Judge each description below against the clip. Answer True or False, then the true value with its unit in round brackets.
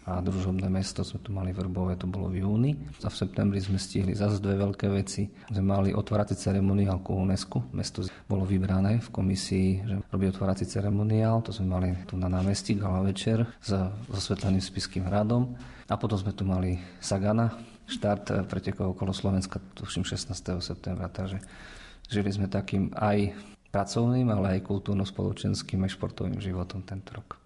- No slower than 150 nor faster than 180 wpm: True (160 wpm)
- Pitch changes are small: True (1.6 semitones)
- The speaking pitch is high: False (100 Hz)